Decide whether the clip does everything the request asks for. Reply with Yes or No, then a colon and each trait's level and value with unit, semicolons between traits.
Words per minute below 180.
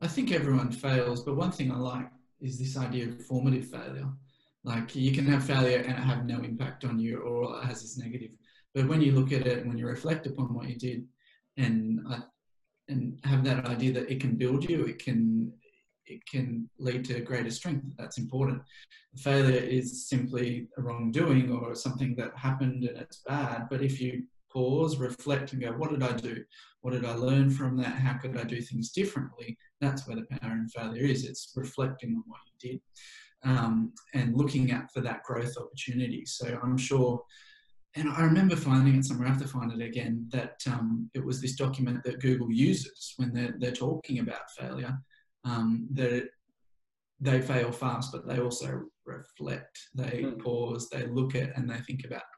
No: average, 195 wpm